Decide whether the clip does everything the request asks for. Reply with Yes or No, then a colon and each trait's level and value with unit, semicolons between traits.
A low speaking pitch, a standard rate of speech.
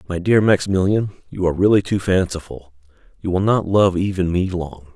Yes: very low, 90 Hz; average, 180 wpm